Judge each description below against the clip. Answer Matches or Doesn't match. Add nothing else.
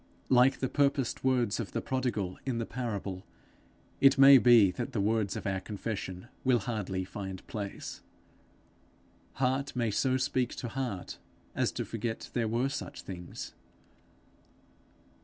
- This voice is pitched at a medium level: Doesn't match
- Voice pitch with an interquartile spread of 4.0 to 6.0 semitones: Matches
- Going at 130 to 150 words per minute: Matches